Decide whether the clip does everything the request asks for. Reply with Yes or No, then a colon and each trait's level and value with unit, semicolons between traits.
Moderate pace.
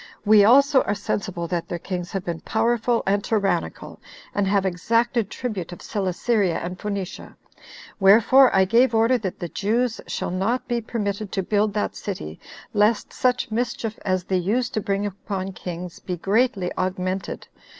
Yes: average, 160 wpm